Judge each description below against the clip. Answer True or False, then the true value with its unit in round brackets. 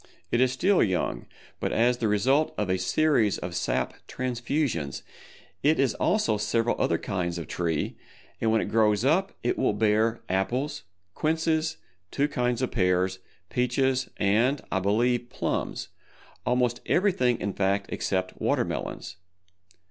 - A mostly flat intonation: False (5.0 semitones)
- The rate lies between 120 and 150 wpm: True (140 wpm)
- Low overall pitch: True (115 Hz)